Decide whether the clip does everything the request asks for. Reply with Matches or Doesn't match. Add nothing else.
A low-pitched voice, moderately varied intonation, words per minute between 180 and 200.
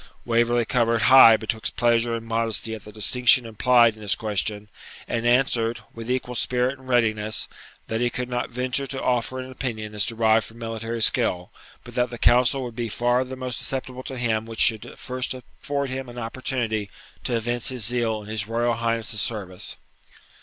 Doesn't match